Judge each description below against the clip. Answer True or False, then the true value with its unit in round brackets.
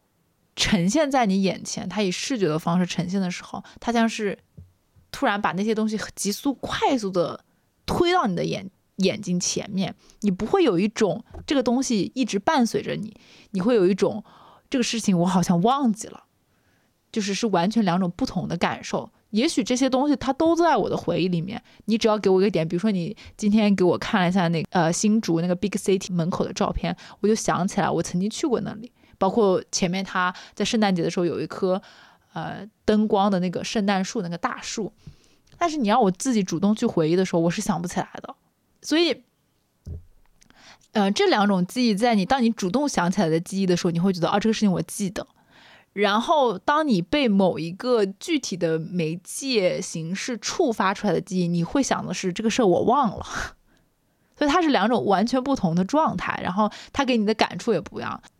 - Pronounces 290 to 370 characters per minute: True (305 characters per minute)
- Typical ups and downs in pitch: True (4.2 semitones)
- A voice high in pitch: True (200 Hz)